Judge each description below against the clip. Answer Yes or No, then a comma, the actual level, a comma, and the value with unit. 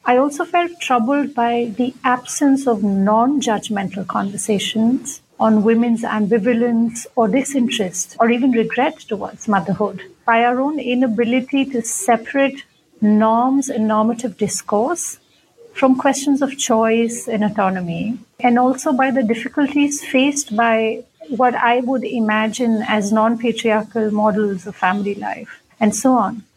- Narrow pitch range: No, average, 3.3 semitones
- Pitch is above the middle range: Yes, high, 235 Hz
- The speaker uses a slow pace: Yes, slow, 130 wpm